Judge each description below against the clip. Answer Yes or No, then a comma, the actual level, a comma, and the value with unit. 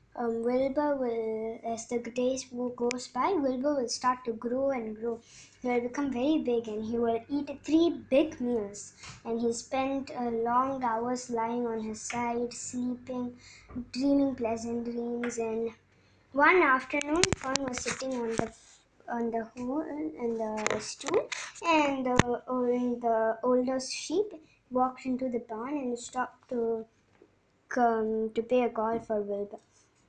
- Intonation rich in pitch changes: No, narrow, 2.4 semitones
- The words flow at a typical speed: No, fast, 150 wpm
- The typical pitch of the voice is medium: No, high, 245 Hz